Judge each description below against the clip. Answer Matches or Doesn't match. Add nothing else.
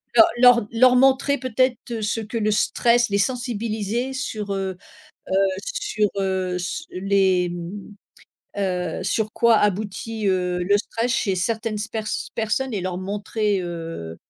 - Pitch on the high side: Matches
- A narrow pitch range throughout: Doesn't match